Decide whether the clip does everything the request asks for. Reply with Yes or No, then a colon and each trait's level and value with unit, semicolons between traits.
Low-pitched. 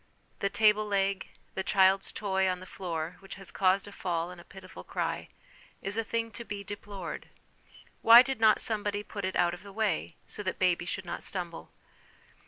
No: high, 195 Hz